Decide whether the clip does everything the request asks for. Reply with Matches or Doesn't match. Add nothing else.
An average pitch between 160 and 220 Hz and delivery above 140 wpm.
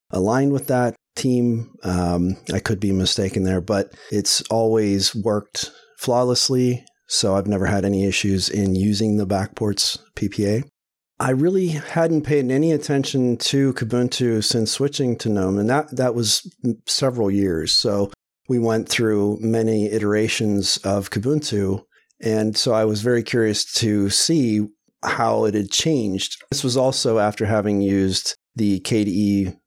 Doesn't match